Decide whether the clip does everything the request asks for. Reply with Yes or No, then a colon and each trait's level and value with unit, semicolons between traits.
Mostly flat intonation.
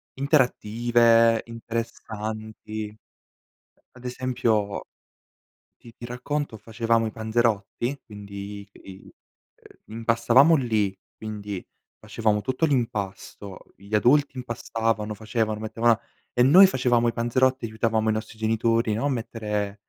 Yes: narrow, 2.1 semitones